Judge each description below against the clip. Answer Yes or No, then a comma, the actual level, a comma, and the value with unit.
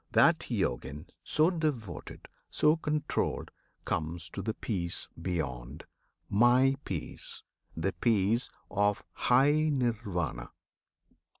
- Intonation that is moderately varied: No, wide, 7.9 semitones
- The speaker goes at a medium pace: No, slow, 95 wpm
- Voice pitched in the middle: No, low, 105 Hz